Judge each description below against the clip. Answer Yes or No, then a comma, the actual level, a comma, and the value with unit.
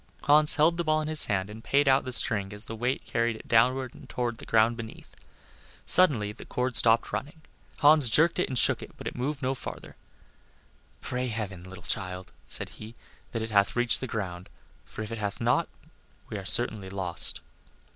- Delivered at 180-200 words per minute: Yes, average, 195 wpm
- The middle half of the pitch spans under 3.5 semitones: No, average, 4.2 semitones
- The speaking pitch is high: No, low, 115 Hz